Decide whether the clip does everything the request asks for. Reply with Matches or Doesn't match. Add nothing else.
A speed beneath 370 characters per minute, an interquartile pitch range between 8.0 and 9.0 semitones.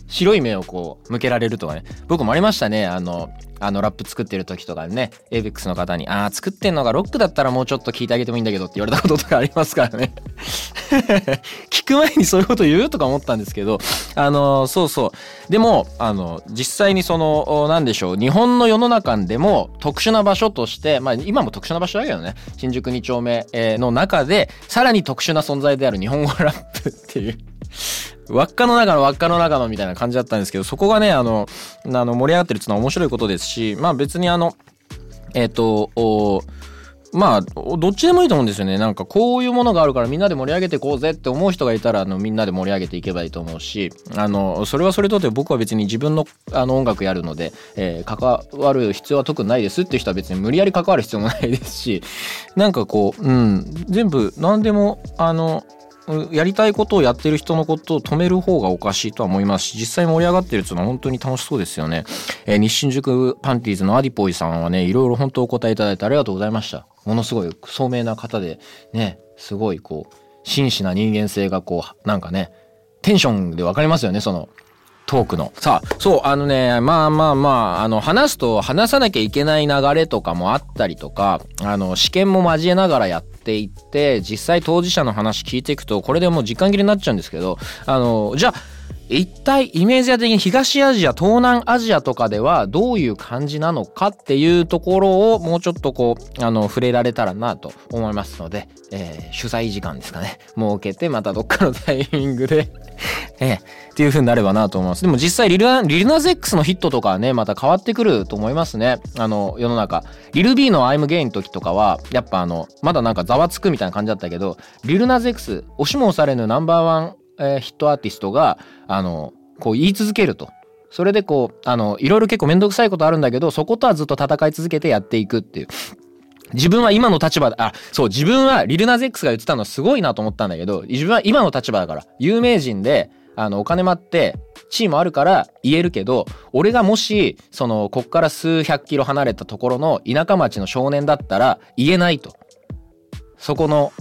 Doesn't match